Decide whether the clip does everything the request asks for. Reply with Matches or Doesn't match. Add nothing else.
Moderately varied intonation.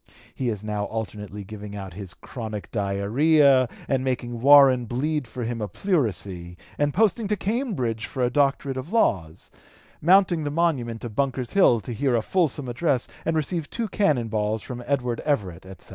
Doesn't match